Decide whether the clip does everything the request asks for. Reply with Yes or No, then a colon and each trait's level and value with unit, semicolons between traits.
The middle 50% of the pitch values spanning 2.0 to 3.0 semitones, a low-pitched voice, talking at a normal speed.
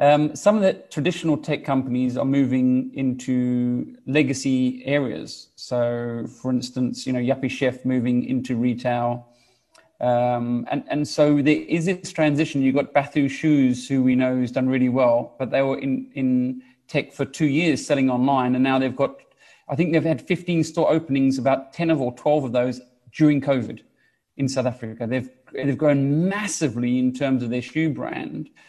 Yes: average, 2.7 semitones; low, 130 Hz; average, 180 wpm